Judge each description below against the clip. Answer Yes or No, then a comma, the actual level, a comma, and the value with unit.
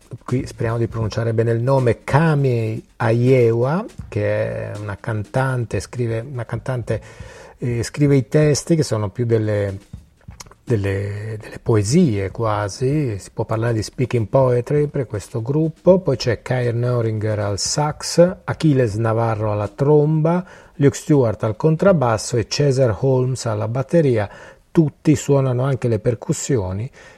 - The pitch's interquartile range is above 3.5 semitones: Yes, average, 4.0 semitones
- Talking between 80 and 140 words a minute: Yes, average, 135 wpm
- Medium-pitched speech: No, low, 120 Hz